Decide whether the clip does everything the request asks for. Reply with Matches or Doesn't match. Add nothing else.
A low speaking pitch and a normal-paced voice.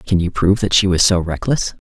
Doesn't match